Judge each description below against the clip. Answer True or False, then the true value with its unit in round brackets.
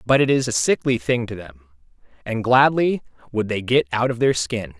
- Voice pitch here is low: True (115 Hz)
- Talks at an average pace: False (215 wpm)